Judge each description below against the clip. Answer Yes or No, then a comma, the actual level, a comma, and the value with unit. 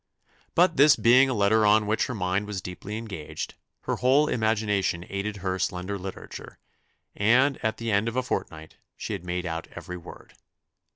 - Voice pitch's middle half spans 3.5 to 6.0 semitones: Yes, average, 3.9 semitones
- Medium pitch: No, low, 105 Hz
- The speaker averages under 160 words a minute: No, average, 175 wpm